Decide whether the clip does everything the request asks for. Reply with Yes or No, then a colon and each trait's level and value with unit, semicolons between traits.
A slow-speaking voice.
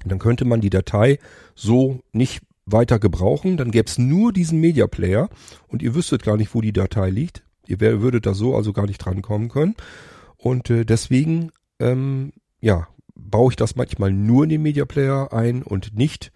No: average, 185 wpm